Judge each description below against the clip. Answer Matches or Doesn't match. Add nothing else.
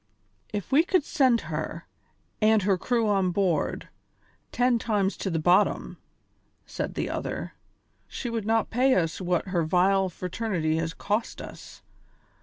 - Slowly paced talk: Doesn't match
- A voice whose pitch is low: Doesn't match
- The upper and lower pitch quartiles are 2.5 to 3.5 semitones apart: Doesn't match